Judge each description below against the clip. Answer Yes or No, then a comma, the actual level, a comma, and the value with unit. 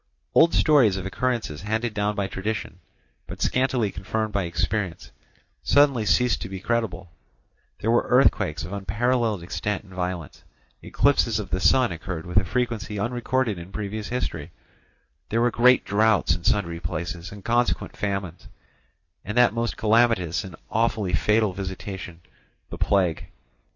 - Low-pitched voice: Yes, low, 105 Hz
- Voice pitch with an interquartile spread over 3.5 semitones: Yes, average, 4.3 semitones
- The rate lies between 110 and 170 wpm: Yes, average, 145 wpm